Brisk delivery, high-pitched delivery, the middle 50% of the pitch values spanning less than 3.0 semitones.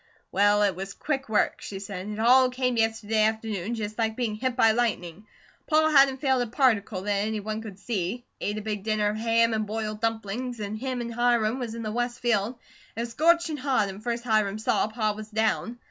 Yes: fast, 215 wpm; high, 220 Hz; narrow, 2.5 semitones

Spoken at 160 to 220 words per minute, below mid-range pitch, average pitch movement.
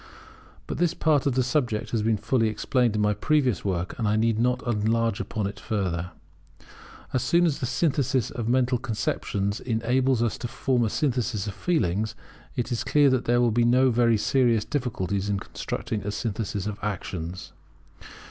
Yes: average, 180 wpm; low, 115 Hz; average, 3.4 semitones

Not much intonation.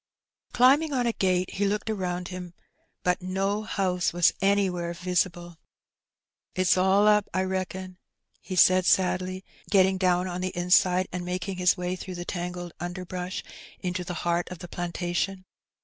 Yes: narrow, 1.2 semitones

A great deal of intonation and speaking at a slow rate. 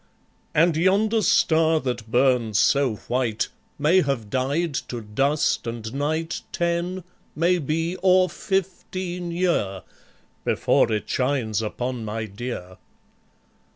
Yes: wide, 6.9 semitones; slow, 110 wpm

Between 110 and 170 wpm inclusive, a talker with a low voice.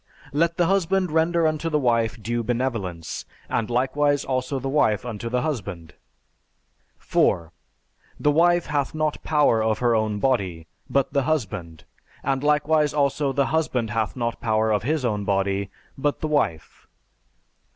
Yes: average, 150 wpm; low, 130 Hz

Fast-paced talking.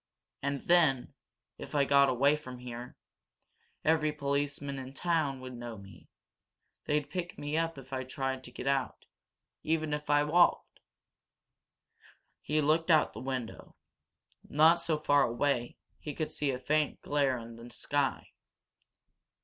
No: average, 150 wpm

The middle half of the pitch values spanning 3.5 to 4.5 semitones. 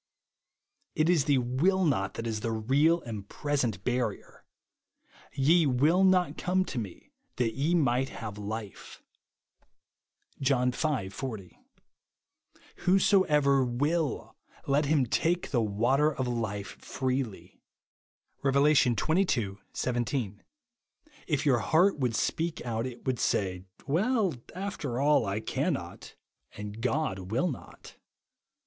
No: wide, 5.4 semitones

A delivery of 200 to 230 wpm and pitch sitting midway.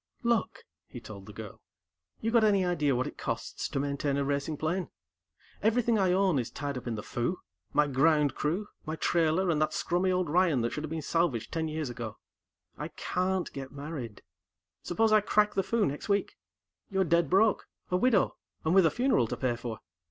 Yes: fast, 205 wpm; medium, 165 Hz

